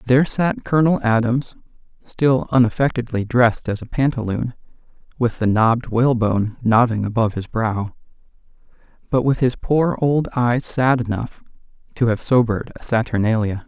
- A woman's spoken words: No, male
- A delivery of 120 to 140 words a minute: Yes, slow, 135 wpm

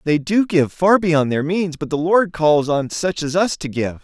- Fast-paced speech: Yes, fast, 255 wpm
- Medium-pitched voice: Yes, medium, 160 Hz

